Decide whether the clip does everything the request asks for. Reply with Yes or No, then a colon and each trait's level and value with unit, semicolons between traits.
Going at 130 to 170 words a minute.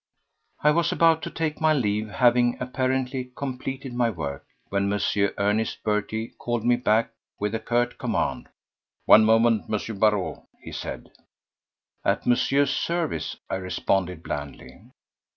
Yes: slow, 135 wpm